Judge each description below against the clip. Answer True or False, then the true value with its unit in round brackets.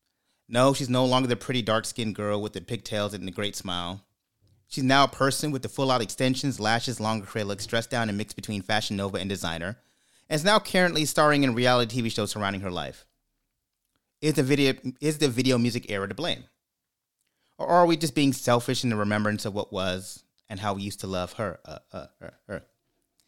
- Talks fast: True (210 wpm)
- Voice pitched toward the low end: True (115 Hz)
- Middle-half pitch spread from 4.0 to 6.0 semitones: True (4.4 semitones)